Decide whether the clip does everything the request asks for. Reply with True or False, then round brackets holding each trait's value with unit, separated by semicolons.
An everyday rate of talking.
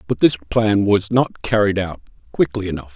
True (185 wpm)